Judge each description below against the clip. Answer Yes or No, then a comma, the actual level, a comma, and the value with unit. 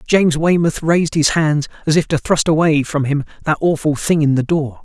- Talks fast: Yes, fast, 225 wpm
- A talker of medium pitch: Yes, medium, 155 Hz